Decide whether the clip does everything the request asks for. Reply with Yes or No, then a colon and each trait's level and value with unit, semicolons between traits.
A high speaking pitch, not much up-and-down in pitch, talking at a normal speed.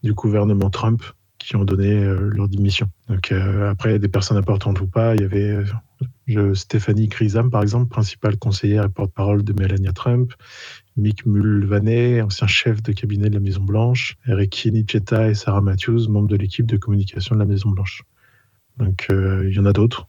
No: low, 105 Hz; narrow, 2.1 semitones; average, 195 wpm